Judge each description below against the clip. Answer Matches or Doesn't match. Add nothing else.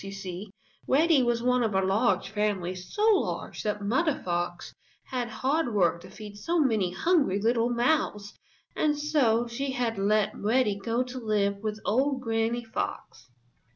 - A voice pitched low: Doesn't match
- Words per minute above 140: Matches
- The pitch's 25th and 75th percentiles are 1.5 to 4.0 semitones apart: Doesn't match